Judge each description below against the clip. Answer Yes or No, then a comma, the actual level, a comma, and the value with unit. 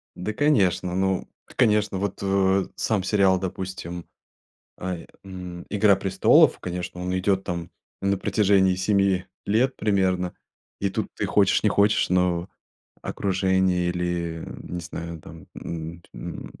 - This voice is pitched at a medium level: No, very low, 95 Hz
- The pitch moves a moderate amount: No, narrow, 1.9 semitones